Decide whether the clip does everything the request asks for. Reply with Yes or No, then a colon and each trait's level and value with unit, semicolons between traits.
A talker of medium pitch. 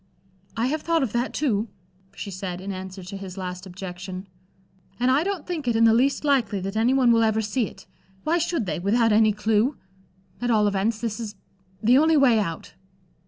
No: high, 220 Hz